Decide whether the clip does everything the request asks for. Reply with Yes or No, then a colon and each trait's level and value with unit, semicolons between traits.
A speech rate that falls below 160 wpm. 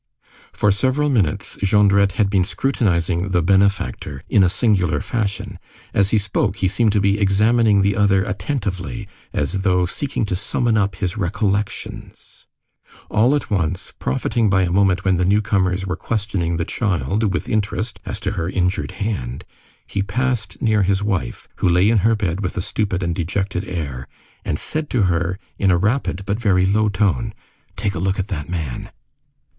No: average, 175 wpm